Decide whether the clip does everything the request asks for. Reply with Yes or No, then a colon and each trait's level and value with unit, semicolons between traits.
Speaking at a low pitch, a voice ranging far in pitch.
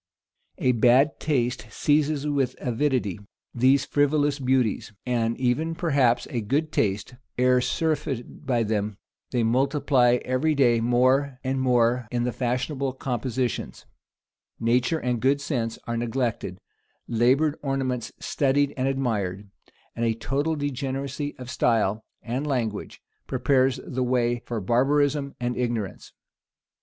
No: low, 125 Hz; average, 2.8 semitones